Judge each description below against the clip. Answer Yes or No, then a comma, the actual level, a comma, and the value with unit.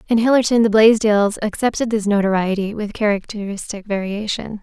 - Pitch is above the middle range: Yes, high, 210 Hz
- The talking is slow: Yes, slow, 130 wpm